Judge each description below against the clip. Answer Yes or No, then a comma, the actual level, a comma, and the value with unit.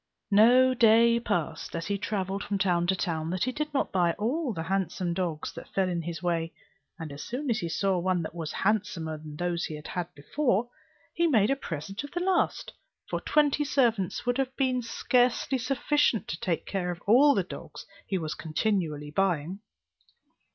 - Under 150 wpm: No, average, 190 wpm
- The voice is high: Yes, high, 195 Hz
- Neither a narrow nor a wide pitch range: No, wide, 6.2 semitones